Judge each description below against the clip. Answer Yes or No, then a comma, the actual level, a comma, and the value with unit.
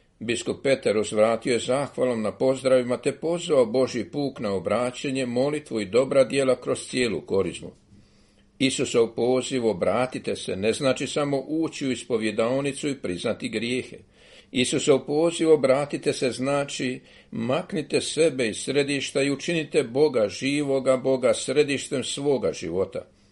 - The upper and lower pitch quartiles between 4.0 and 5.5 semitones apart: No, average, 2.8 semitones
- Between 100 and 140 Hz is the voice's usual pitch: Yes, low, 135 Hz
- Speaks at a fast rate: No, average, 130 wpm